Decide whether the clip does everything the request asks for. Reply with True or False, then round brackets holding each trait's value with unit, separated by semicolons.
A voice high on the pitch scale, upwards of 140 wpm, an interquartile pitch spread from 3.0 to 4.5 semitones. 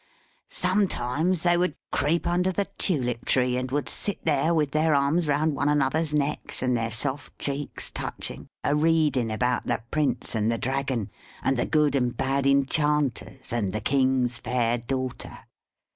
False (140 Hz; 160 wpm; 3.5 semitones)